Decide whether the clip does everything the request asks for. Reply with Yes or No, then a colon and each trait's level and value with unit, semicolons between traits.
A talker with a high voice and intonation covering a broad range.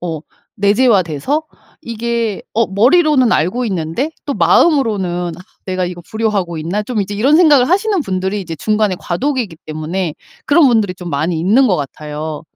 Yes: high, 200 Hz; wide, 6.1 semitones